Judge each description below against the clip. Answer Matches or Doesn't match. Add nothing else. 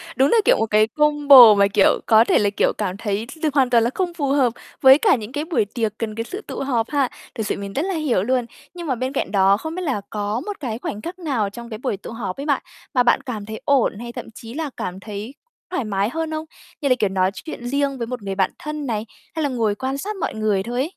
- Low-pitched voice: Doesn't match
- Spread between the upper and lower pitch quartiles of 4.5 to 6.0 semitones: Matches